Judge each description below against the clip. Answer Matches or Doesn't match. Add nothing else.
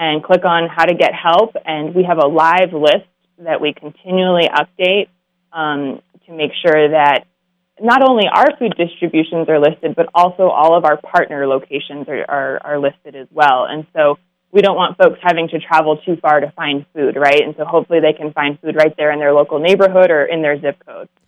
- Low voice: Doesn't match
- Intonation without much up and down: Doesn't match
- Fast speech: Matches